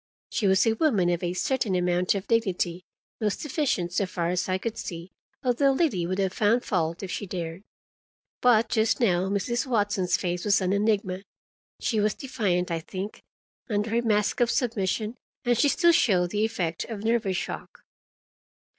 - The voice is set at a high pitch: Yes, high, 205 Hz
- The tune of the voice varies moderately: Yes, average, 4.1 semitones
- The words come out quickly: No, average, 175 wpm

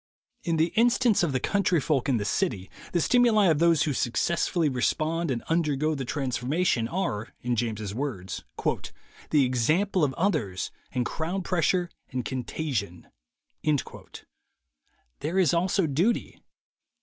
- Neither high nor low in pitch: Yes, medium, 155 Hz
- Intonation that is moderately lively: No, wide, 6.0 semitones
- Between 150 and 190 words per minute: No, slow, 135 wpm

